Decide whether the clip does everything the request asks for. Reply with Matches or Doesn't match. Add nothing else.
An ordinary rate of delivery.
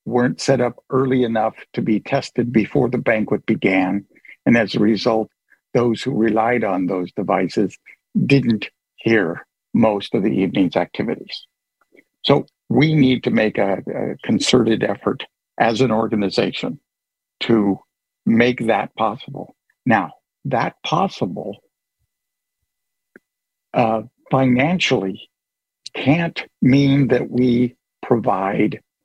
Doesn't match